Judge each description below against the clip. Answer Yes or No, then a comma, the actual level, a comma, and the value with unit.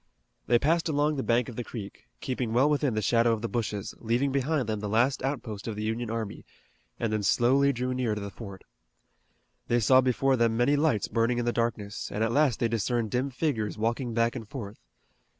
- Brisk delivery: Yes, fast, 215 wpm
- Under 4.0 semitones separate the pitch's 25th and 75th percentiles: Yes, average, 2.9 semitones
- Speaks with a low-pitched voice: Yes, low, 120 Hz